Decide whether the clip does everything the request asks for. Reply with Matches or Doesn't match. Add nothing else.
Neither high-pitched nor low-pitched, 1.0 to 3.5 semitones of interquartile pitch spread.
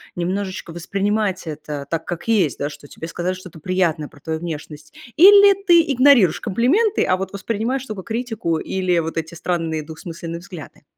Doesn't match